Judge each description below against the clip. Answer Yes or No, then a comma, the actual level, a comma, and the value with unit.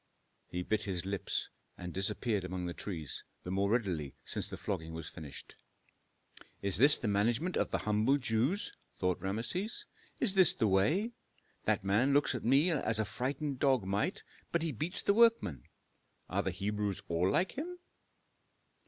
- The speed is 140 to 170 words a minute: Yes, average, 165 wpm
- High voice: No, low, 105 Hz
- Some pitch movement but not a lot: No, wide, 7.0 semitones